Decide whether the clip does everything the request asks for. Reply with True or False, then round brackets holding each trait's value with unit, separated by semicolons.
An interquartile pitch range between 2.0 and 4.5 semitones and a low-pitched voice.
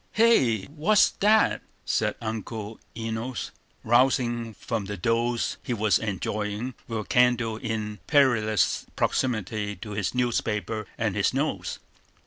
True (2.6 semitones; 115 Hz)